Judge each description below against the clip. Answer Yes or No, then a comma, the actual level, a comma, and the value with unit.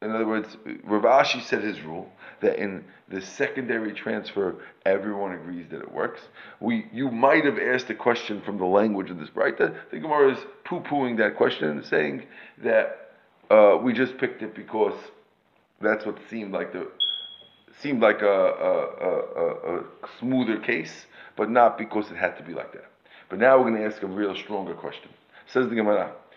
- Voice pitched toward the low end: Yes, low, 115 Hz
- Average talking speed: Yes, average, 185 wpm